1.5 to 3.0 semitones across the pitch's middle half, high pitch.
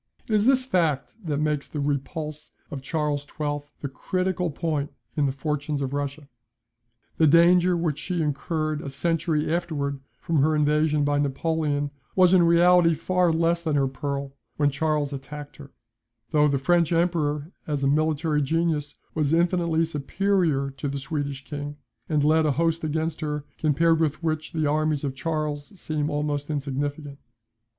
No: narrow, 2.4 semitones; medium, 150 Hz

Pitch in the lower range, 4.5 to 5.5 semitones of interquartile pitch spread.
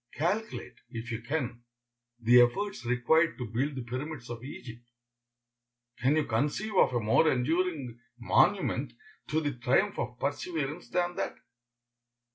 Yes: low, 130 Hz; average, 4.9 semitones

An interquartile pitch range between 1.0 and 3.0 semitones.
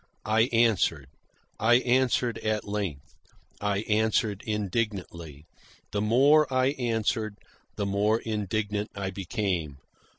Yes: narrow, 2.6 semitones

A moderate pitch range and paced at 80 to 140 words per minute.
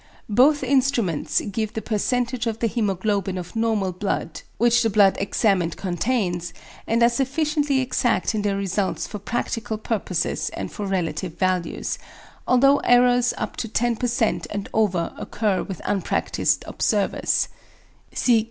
Yes: average, 4.0 semitones; slow, 135 wpm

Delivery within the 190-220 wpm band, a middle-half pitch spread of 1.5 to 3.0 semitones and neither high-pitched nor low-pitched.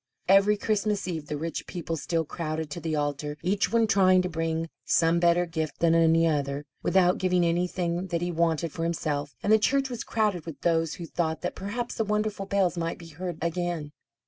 Yes: average, 200 wpm; average, 2.7 semitones; medium, 170 Hz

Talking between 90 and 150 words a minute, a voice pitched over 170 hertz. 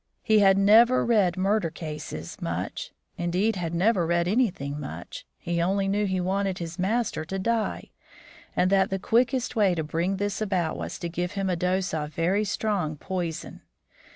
No: average, 175 wpm; high, 190 Hz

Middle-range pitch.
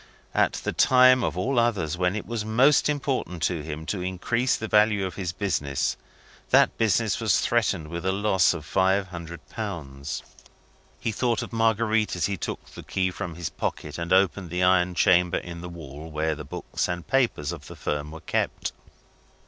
No: very low, 95 Hz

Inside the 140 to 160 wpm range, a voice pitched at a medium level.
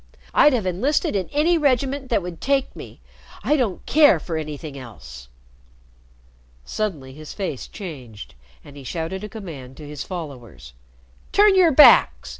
Yes: average, 150 wpm; medium, 180 Hz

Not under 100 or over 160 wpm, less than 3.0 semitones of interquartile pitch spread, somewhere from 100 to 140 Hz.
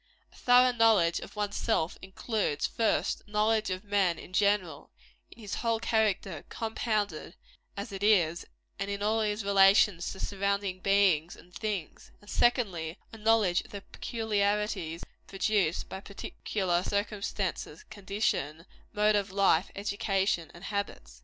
No: average, 140 wpm; narrow, 2.5 semitones; high, 200 Hz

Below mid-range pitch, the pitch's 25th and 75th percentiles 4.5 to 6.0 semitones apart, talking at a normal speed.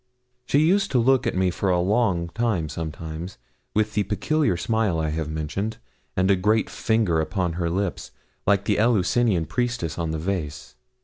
Yes: very low, 95 Hz; average, 5.1 semitones; average, 175 wpm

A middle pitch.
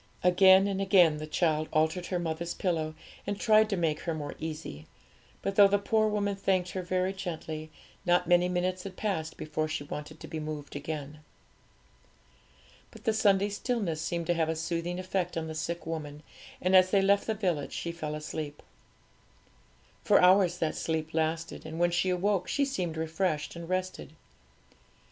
Yes: medium, 175 Hz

